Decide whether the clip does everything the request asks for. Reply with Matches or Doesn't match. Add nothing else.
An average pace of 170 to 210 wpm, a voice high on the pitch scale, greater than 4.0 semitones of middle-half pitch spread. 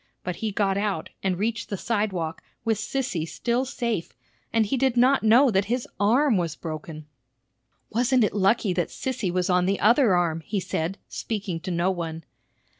Matches